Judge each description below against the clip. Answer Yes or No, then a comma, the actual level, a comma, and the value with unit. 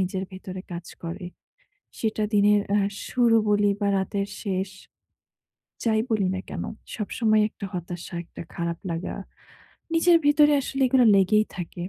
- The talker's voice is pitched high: Yes, high, 205 Hz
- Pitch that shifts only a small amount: No, average, 3.3 semitones